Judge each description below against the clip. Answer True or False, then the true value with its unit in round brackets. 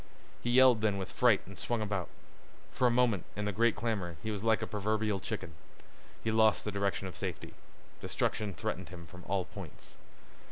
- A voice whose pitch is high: False (105 Hz)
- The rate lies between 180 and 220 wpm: True (190 wpm)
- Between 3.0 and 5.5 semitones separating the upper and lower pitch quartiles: False (2.5 semitones)